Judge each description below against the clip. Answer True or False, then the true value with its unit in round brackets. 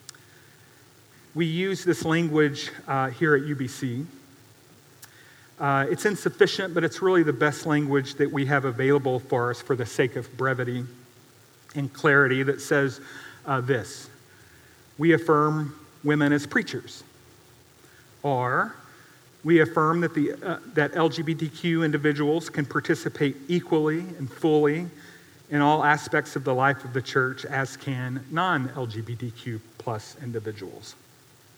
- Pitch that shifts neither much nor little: True (3.3 semitones)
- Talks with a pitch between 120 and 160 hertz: True (140 Hz)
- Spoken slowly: True (125 wpm)